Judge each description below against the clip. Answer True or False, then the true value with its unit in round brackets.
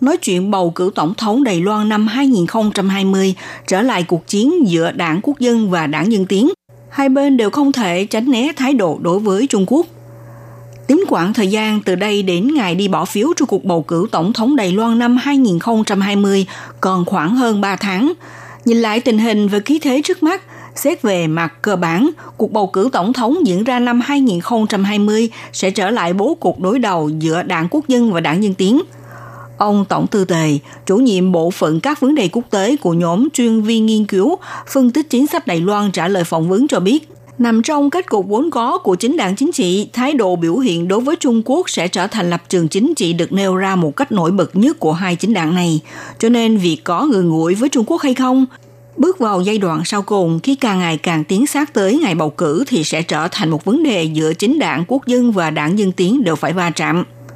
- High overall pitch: True (205 Hz)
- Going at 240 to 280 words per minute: False (225 wpm)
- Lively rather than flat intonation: True (6.1 semitones)